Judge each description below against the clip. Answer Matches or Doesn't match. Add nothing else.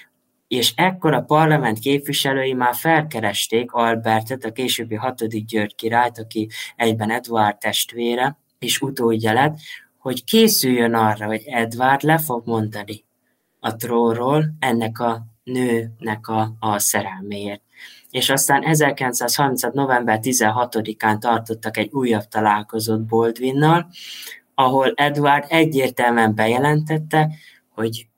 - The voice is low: Matches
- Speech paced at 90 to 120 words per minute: Matches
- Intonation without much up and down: Doesn't match